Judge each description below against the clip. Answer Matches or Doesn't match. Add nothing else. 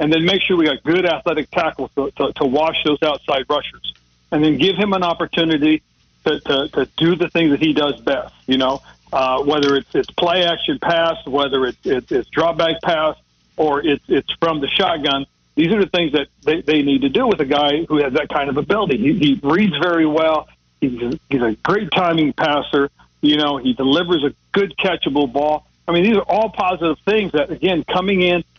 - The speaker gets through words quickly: Matches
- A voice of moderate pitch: Matches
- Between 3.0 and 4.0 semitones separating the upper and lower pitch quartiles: Matches